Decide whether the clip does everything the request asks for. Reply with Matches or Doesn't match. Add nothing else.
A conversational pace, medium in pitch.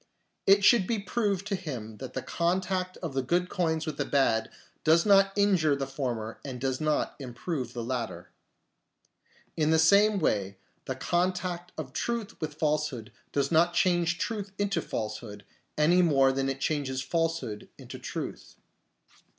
Matches